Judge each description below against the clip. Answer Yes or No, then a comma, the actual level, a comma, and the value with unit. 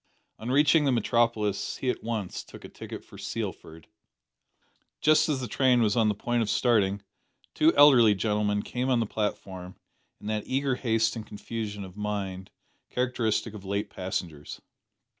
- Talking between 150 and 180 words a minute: Yes, average, 160 wpm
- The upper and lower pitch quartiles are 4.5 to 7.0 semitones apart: No, average, 3.4 semitones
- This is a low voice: Yes, low, 110 Hz